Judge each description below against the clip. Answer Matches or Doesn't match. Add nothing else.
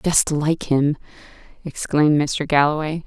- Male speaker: Doesn't match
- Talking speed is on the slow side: Matches